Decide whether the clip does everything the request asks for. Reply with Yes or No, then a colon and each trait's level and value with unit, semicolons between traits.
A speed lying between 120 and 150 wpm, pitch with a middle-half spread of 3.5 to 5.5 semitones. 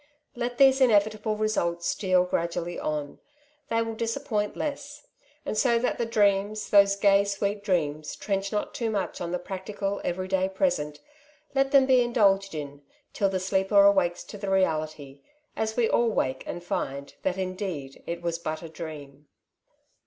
No: average, 165 wpm; average, 4.1 semitones